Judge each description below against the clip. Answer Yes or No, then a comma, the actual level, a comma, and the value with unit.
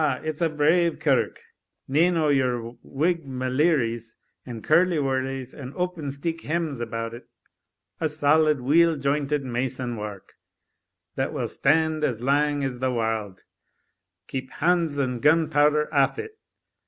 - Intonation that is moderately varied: Yes, average, 3.8 semitones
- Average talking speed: No, slow, 130 wpm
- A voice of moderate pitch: Yes, medium, 145 Hz